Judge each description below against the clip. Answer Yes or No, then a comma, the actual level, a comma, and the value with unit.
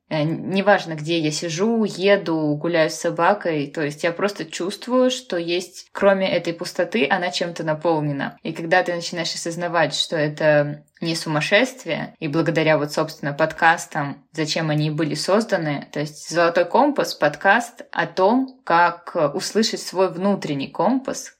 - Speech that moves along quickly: No, average, 145 wpm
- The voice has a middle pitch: Yes, medium, 170 Hz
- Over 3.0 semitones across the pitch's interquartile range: Yes, average, 3.6 semitones